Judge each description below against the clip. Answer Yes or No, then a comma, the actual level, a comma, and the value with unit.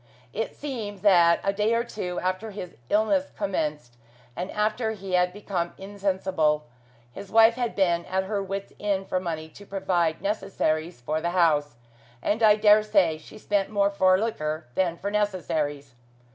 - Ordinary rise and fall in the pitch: Yes, average, 3.5 semitones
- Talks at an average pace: Yes, average, 165 wpm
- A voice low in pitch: No, high, 190 Hz